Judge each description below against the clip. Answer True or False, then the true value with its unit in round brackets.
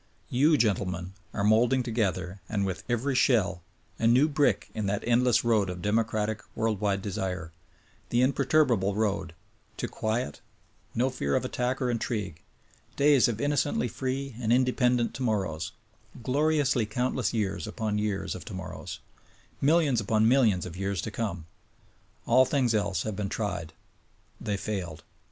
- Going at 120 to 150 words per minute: True (145 wpm)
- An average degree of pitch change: True (4.3 semitones)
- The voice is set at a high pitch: False (110 Hz)